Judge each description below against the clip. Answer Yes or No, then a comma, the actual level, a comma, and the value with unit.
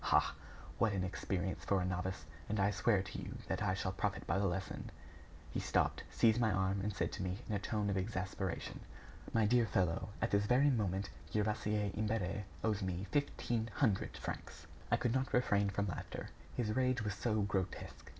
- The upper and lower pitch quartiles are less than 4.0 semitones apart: Yes, average, 2.7 semitones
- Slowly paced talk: No, average, 190 wpm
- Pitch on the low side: Yes, low, 100 Hz